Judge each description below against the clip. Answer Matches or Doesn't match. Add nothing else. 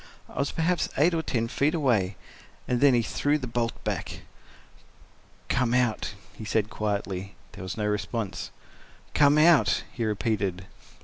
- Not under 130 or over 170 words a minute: Matches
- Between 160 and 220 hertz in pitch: Doesn't match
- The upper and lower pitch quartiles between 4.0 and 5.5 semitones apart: Matches